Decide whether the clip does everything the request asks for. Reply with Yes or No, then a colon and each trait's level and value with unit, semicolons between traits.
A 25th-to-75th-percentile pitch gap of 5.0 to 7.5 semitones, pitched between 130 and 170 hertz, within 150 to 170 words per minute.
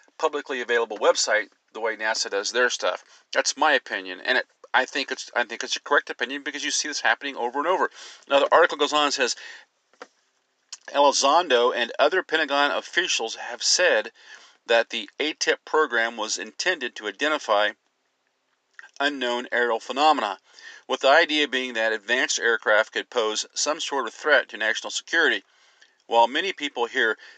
Yes: average, 5.3 semitones; medium, 140 Hz; average, 165 wpm